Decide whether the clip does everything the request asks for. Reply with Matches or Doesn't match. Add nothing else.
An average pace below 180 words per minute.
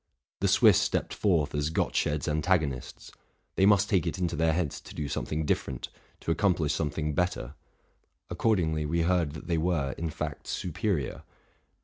Matches